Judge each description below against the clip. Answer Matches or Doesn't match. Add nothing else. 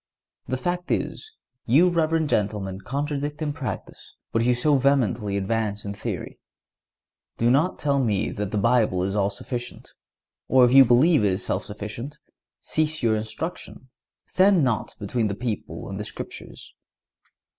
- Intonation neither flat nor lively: Doesn't match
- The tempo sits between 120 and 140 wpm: Doesn't match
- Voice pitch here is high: Doesn't match